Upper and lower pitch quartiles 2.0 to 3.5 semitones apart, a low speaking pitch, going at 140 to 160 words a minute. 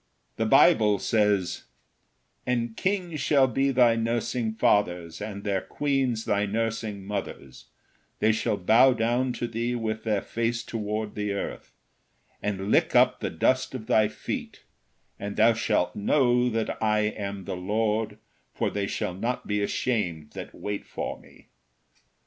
Yes: narrow, 2.5 semitones; low, 110 Hz; average, 150 wpm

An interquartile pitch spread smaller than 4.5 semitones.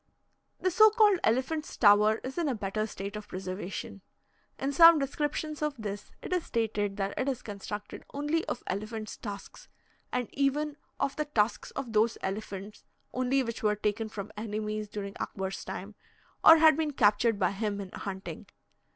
No: wide, 5.4 semitones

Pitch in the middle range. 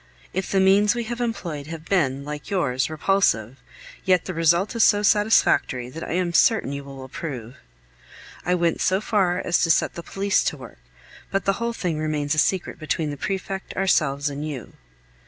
Yes: medium, 170 Hz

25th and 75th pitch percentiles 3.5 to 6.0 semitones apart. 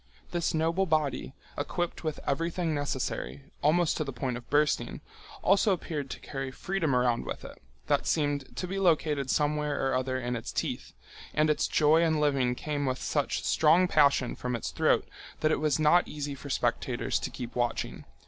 No: average, 3.1 semitones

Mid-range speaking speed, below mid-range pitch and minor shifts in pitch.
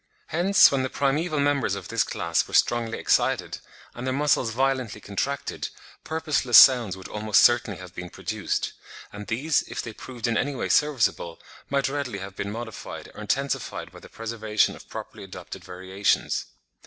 No: average, 165 wpm; low, 120 Hz; average, 5.1 semitones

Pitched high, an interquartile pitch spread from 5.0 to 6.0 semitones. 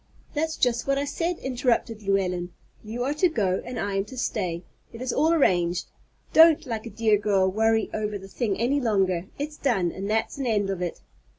Yes: high, 220 Hz; average, 5.3 semitones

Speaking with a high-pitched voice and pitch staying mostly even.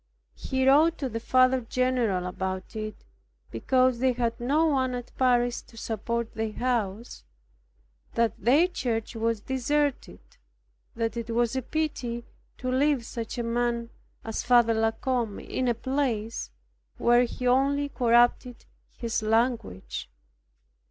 Yes: high, 240 Hz; narrow, 2.2 semitones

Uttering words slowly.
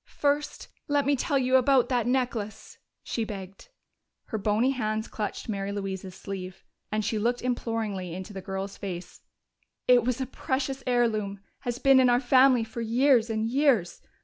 No: average, 165 wpm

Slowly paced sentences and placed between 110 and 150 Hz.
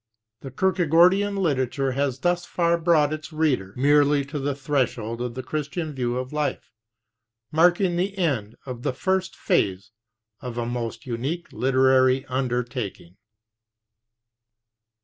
Yes: slow, 130 wpm; medium, 140 Hz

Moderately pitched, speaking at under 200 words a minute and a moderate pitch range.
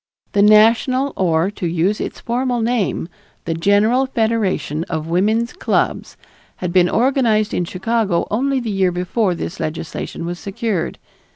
No: high, 205 Hz; average, 145 wpm; average, 4.8 semitones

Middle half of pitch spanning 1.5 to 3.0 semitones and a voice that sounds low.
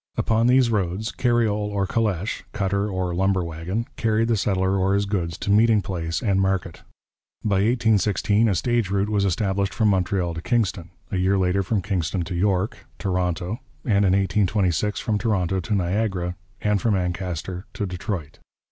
Yes: narrow, 2.6 semitones; low, 100 Hz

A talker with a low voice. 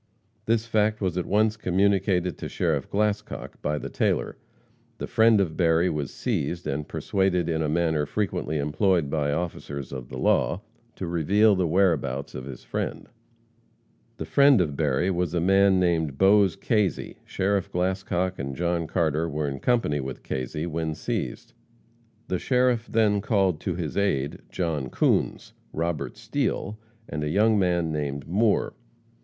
Yes: very low, 90 Hz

